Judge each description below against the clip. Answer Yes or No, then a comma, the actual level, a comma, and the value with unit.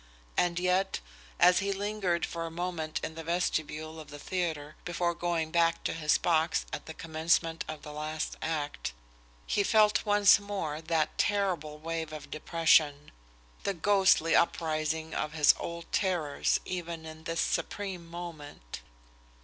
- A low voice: No, medium, 165 Hz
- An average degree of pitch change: No, narrow, 2.3 semitones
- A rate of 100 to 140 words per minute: No, average, 150 wpm